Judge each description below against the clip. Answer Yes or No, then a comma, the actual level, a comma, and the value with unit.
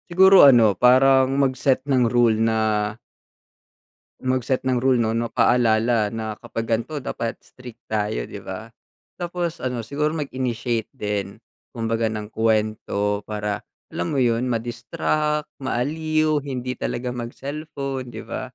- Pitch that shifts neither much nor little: Yes, average, 3.3 semitones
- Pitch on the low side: Yes, low, 125 Hz